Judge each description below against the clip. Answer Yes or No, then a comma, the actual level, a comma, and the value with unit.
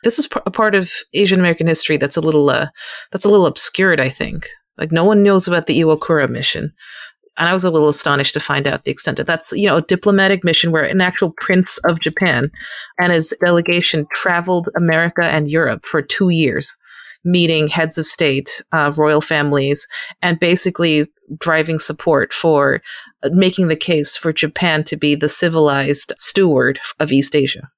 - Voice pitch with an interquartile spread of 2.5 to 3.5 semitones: Yes, average, 3.1 semitones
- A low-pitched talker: No, medium, 165 Hz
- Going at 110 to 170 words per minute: No, average, 185 wpm